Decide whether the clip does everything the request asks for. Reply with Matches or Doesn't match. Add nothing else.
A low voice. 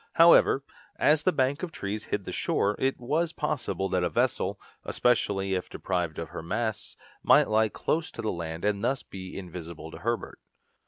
Matches